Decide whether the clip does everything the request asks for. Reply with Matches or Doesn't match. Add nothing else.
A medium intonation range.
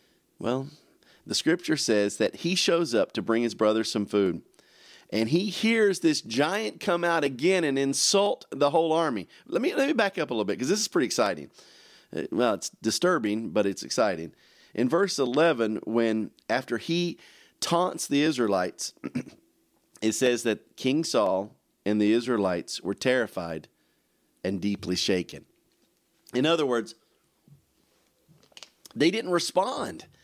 Doesn't match